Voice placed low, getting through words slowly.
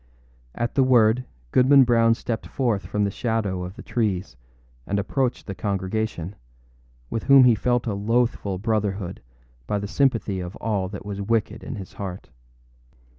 No: low, 110 Hz; average, 160 wpm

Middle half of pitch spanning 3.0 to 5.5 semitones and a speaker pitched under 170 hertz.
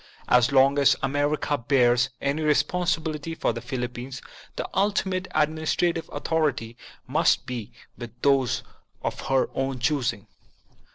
Yes: average, 4.0 semitones; medium, 140 Hz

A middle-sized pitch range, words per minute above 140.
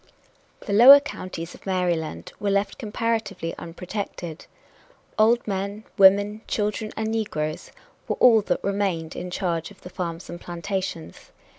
No: average, 3.7 semitones; slow, 135 wpm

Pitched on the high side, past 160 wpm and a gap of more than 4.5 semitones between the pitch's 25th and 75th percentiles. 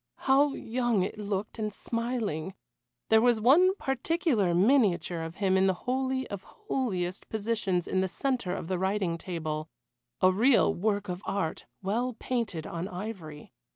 No: high, 205 Hz; average, 155 wpm; average, 5.2 semitones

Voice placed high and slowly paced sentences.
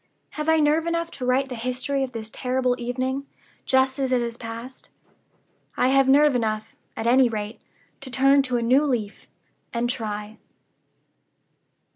No: very high, 255 Hz; average, 160 wpm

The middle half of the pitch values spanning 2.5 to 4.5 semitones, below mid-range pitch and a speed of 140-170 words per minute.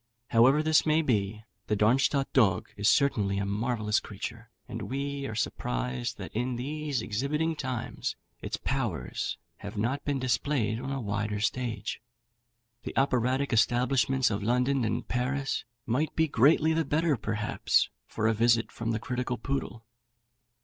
Yes: average, 4.2 semitones; low, 120 Hz; average, 150 wpm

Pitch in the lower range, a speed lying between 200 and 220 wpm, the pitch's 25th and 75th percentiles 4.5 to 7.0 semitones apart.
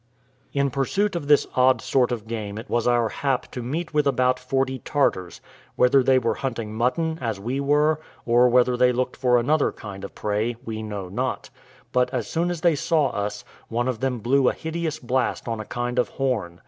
No: low, 125 Hz; fast, 205 wpm; average, 3.2 semitones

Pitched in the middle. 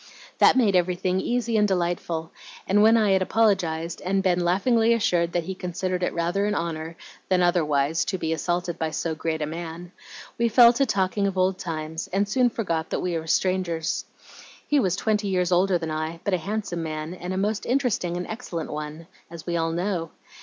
Yes: medium, 180 Hz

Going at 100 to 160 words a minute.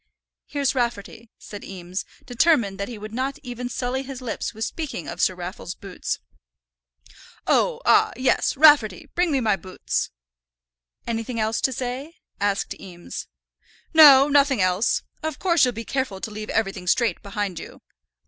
Yes: average, 155 wpm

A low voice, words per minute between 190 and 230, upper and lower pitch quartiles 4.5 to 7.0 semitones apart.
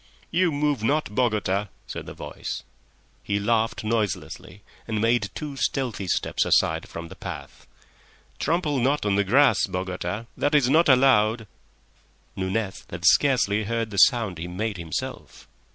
No: low, 110 Hz; average, 145 wpm; wide, 5.4 semitones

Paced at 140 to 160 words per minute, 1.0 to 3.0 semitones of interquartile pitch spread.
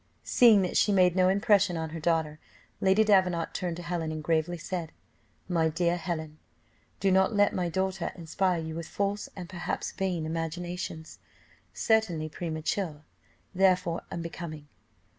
Yes: average, 145 wpm; average, 2.7 semitones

